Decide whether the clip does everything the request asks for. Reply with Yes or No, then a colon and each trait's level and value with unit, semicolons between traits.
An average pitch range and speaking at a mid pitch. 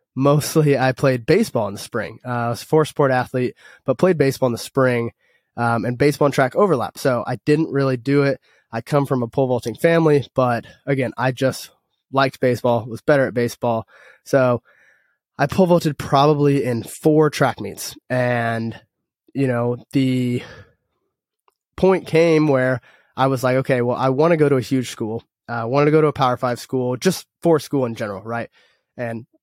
No: average, 3.1 semitones; low, 130 Hz